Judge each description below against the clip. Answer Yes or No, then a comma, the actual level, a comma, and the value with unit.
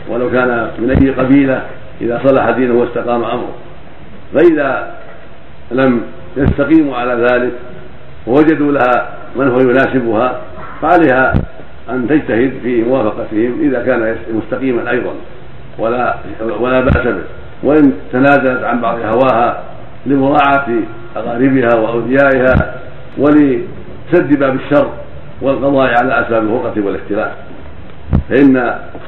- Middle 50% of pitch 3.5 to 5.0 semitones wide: No, narrow, 2.4 semitones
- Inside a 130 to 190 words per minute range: No, average, 105 wpm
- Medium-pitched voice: No, low, 130 Hz